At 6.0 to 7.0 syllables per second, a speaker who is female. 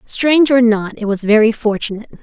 Yes: 6.1 syllables/s; female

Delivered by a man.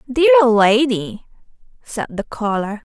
No: female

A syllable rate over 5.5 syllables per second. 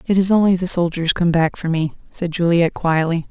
Yes: 5.7 syllables/s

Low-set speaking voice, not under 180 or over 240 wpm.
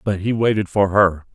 Yes: low, 100 Hz; fast, 225 wpm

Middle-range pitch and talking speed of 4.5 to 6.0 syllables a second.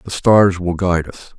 No: very low, 90 Hz; 5.0 syllables/s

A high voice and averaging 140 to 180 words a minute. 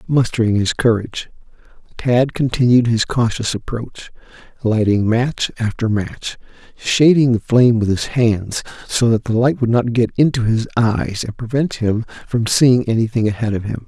No: low, 115 Hz; average, 160 wpm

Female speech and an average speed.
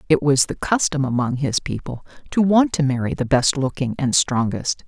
Yes: female; average, 195 wpm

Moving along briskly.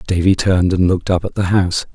Yes: fast, 245 wpm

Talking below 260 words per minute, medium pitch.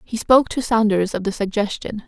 No: average, 200 wpm; high, 215 Hz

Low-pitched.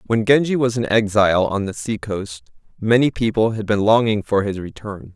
Yes: low, 110 Hz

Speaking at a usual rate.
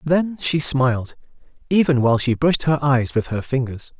Yes: average, 180 wpm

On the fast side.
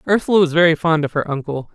Yes: fast, 240 wpm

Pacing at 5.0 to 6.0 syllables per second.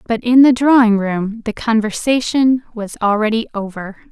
No: 4.6 syllables/s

